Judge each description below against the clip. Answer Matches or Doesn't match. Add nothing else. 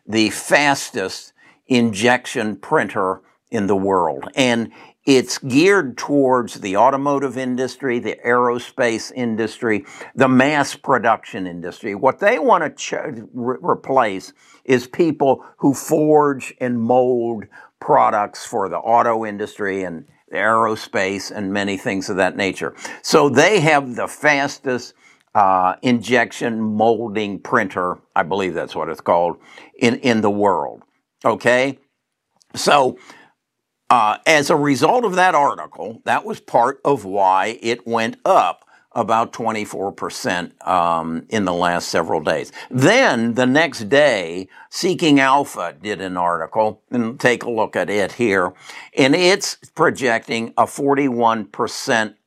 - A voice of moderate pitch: Doesn't match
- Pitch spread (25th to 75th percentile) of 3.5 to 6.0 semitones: Matches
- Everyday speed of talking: Doesn't match